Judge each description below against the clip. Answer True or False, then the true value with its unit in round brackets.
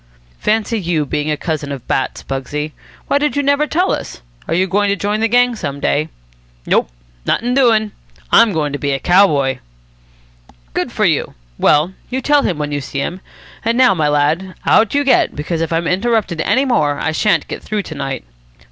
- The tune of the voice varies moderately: False (7.6 semitones)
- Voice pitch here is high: False (180 Hz)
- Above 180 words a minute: True (200 wpm)